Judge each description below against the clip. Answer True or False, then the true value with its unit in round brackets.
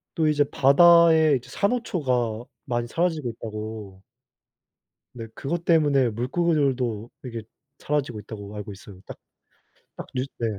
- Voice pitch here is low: True (130 Hz)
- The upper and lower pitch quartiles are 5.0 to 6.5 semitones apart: True (5.6 semitones)